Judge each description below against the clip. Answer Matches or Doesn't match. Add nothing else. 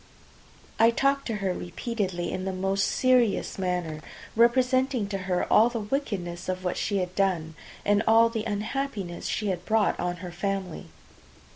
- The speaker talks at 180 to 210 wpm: Doesn't match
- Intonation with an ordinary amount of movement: Matches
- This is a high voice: Matches